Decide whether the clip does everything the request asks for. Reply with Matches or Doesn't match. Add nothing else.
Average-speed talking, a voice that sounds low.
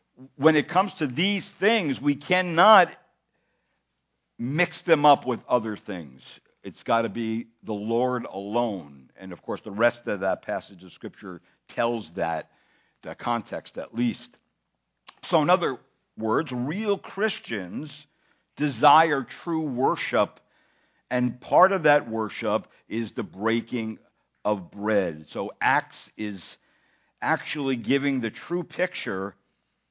Doesn't match